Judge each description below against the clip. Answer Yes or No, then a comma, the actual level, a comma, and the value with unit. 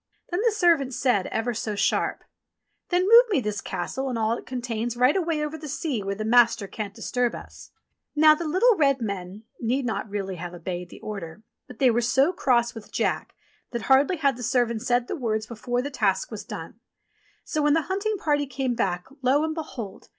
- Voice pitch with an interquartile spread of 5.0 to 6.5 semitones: Yes, wide, 5.4 semitones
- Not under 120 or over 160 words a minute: No, fast, 205 wpm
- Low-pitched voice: No, high, 245 Hz